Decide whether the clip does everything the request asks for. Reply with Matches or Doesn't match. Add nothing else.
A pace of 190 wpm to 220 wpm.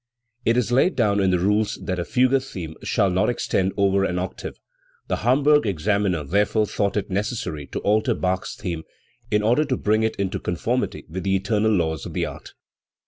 Matches